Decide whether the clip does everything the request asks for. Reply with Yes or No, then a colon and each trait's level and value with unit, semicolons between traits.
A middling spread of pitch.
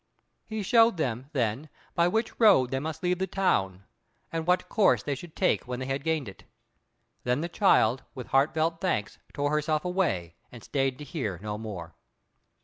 No: wide, 6.0 semitones